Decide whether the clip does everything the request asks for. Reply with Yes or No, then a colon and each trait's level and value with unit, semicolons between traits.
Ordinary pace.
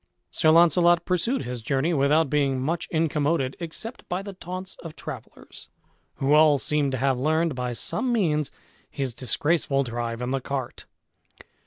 Yes: average, 155 wpm